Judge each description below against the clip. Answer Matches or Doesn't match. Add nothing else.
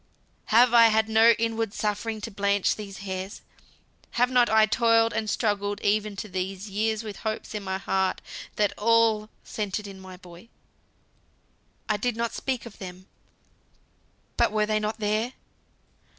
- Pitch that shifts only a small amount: Matches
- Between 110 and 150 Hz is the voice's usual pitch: Doesn't match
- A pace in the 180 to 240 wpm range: Doesn't match